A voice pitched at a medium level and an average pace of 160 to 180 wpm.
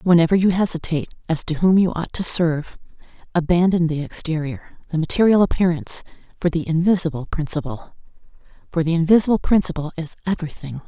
No: medium, 170 Hz; average, 145 wpm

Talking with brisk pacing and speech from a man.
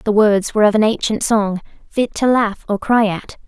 No: fast, 225 wpm; female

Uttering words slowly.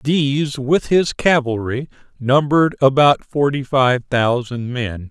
Yes: slow, 120 wpm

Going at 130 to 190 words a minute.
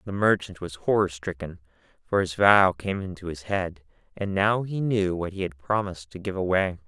No: average, 200 wpm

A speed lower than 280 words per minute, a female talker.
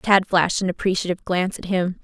Yes: fast, 205 wpm; female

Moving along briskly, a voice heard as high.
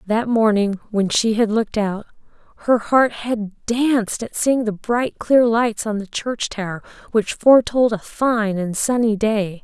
No: average, 175 wpm; high, 220 Hz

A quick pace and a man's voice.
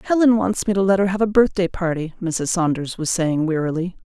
No: fast, 220 wpm; female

